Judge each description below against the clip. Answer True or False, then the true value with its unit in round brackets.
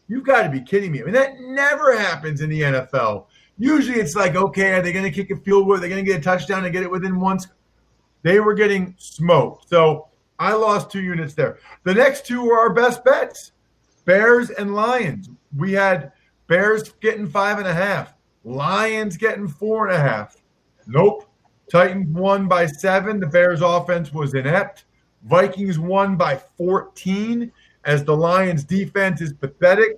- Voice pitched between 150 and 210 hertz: True (190 Hz)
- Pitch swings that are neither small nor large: True (3.2 semitones)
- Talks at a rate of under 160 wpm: False (185 wpm)